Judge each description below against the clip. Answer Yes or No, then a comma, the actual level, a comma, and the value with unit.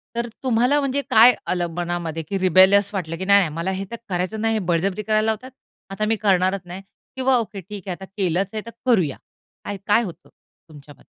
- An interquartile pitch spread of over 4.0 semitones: No, average, 3.7 semitones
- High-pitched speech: Yes, high, 195 Hz